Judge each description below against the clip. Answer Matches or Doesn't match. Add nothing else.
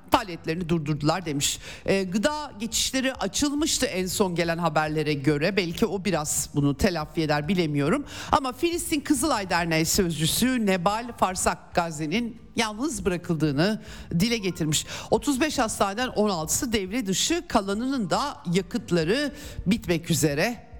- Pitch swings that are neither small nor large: Doesn't match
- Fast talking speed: Doesn't match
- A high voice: Matches